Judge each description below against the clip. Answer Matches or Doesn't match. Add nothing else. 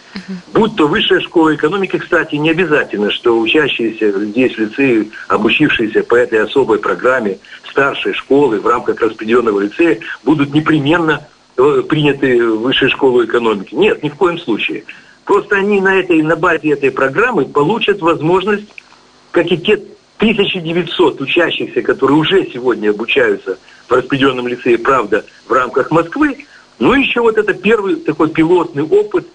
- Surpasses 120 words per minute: Matches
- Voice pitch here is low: Doesn't match